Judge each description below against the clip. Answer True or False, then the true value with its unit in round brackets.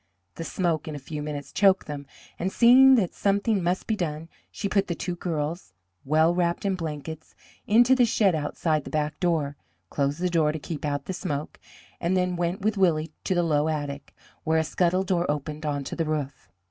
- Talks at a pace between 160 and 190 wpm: False (200 wpm)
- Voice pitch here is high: False (165 Hz)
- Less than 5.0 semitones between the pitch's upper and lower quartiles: True (3.7 semitones)